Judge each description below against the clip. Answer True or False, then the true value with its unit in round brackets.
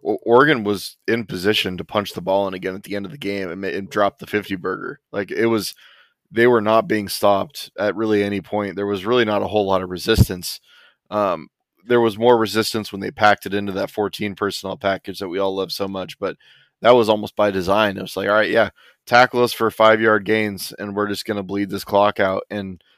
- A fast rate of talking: True (240 wpm)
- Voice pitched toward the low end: True (105 Hz)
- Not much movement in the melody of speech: True (2.0 semitones)